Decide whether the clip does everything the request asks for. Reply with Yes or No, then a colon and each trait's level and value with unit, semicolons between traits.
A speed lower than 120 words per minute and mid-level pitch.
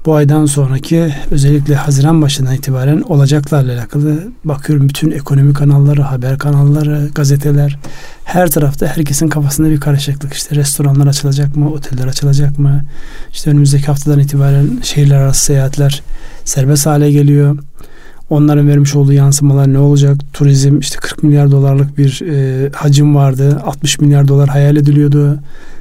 No: average, 135 wpm; medium, 145 Hz